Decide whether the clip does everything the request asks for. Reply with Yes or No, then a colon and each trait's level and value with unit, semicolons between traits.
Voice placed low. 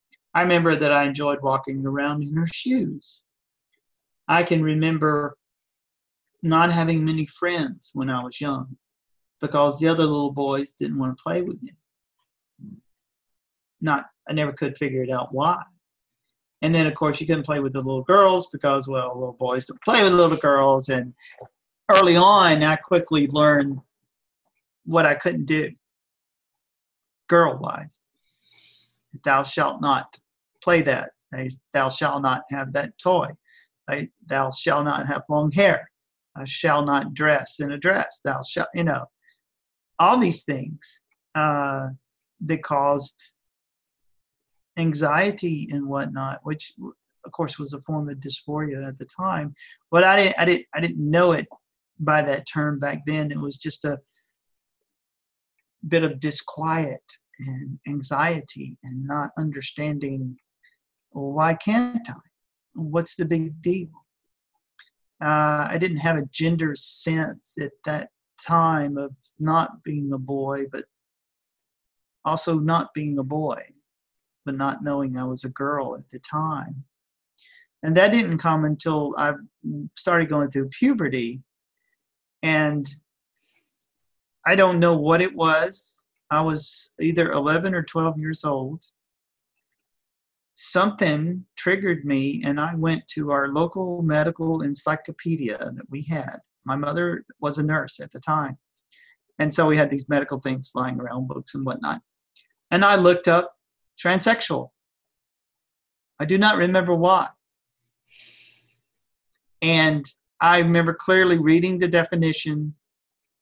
No: medium, 150 Hz